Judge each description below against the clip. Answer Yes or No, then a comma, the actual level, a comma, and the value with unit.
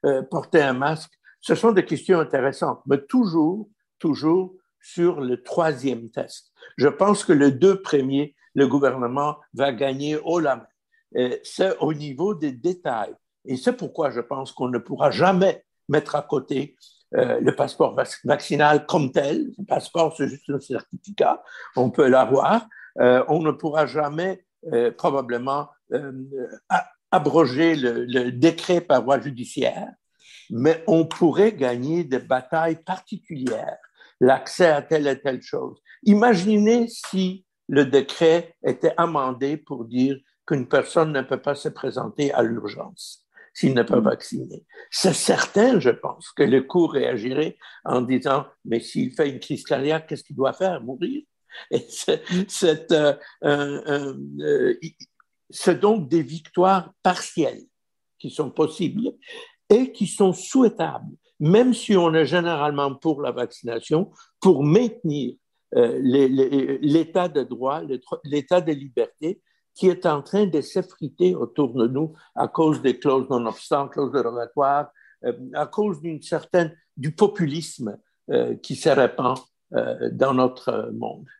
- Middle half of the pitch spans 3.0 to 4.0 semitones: No, average, 5.2 semitones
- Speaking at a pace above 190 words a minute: No, slow, 145 wpm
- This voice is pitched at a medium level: Yes, medium, 155 Hz